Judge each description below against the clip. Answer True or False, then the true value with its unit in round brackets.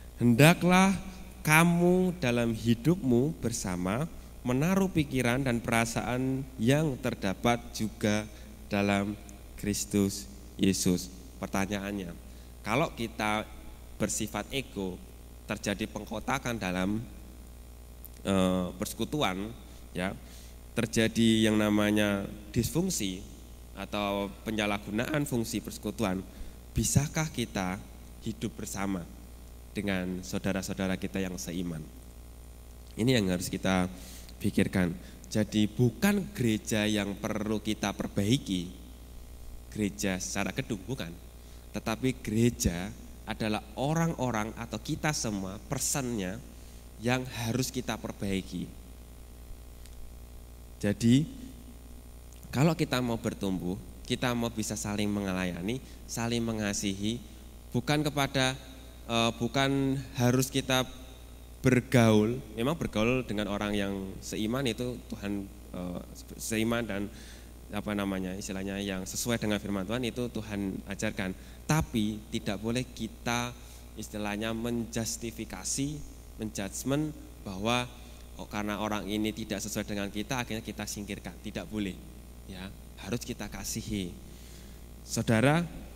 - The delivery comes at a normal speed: True (95 wpm)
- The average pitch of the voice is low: True (105 Hz)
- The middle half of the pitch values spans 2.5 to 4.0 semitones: False (4.6 semitones)